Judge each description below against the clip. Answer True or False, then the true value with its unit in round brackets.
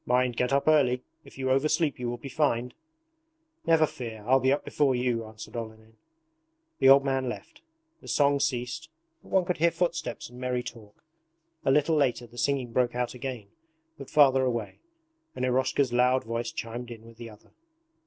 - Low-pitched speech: True (125 Hz)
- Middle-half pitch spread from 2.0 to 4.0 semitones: True (2.7 semitones)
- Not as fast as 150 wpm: False (185 wpm)